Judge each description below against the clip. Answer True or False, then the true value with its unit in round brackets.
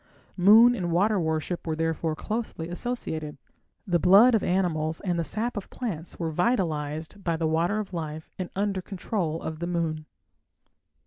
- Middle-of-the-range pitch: True (175 Hz)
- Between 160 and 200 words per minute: True (165 wpm)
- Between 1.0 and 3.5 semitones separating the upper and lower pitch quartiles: False (4.2 semitones)